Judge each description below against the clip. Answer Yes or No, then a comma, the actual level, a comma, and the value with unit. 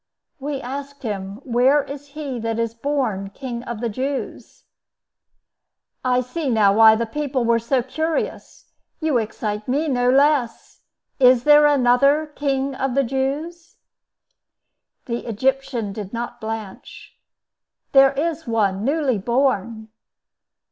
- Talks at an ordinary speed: No, slow, 125 wpm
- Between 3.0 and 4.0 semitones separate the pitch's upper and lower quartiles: Yes, average, 3.6 semitones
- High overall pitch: Yes, very high, 255 Hz